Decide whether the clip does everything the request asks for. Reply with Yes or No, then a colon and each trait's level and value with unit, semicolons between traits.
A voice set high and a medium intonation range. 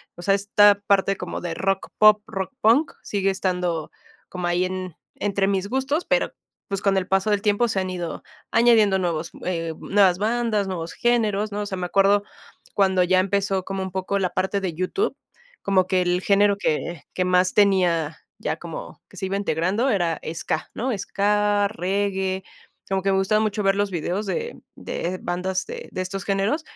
No: high, 195 Hz; narrow, 2.0 semitones